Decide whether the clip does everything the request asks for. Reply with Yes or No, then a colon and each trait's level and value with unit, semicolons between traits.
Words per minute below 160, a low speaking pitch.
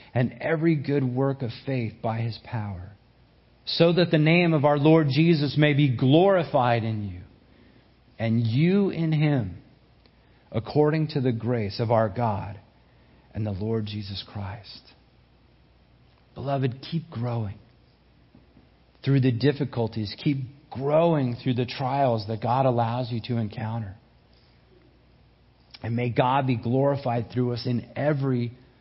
Yes: slow, 135 wpm; low, 120 Hz